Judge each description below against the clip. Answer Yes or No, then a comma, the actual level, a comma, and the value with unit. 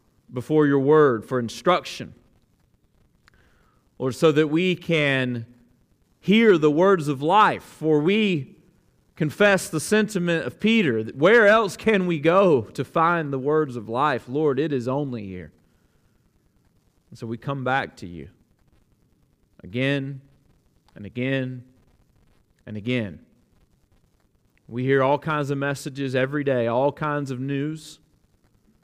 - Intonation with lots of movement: No, average, 4.2 semitones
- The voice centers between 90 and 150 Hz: Yes, medium, 140 Hz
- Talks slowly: Yes, slow, 130 wpm